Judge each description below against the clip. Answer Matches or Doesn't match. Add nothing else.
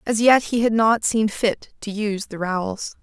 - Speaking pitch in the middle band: Doesn't match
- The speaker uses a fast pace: Matches